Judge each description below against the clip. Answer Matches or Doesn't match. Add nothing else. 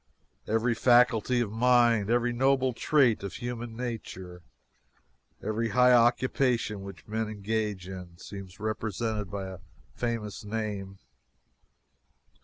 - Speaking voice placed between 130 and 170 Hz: Doesn't match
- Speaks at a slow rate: Matches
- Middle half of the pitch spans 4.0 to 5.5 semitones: Doesn't match